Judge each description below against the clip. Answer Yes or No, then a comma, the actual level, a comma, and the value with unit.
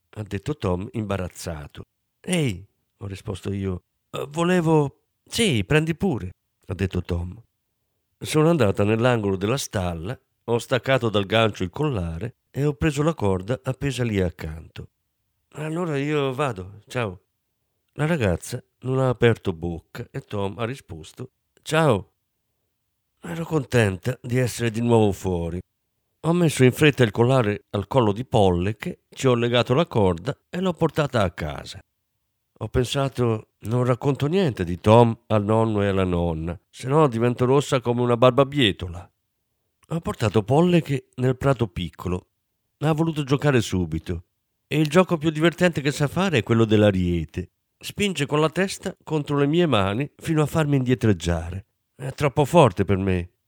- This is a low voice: Yes, low, 120 Hz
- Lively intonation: Yes, wide, 6.4 semitones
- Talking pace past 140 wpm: Yes, average, 155 wpm